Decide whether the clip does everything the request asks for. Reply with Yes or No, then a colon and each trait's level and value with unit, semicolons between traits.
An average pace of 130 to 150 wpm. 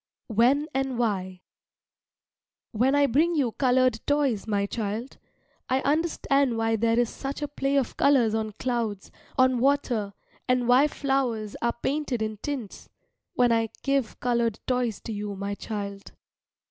Yes: average, 145 wpm